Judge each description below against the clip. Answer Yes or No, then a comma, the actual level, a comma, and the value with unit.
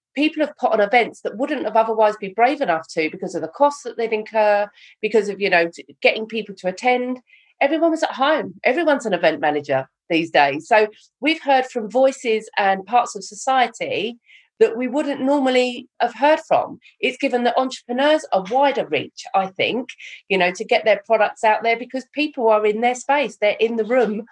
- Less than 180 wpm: No, average, 200 wpm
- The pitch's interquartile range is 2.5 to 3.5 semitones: No, average, 5.1 semitones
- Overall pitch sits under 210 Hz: No, high, 235 Hz